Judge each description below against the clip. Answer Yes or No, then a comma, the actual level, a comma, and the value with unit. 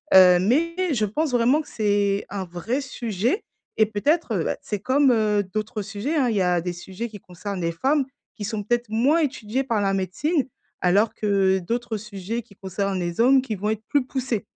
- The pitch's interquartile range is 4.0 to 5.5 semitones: Yes, average, 4.5 semitones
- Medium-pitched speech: No, high, 215 Hz